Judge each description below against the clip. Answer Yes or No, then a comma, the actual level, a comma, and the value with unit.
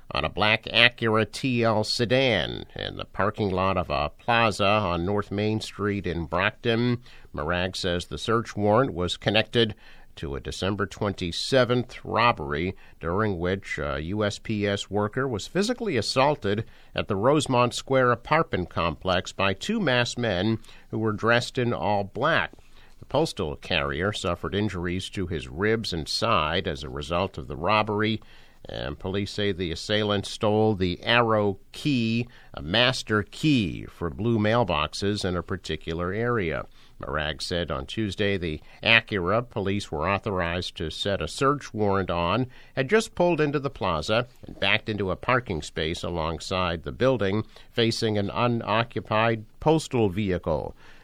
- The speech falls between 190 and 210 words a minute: No, average, 145 wpm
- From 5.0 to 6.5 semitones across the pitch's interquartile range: No, average, 4.5 semitones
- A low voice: Yes, low, 105 Hz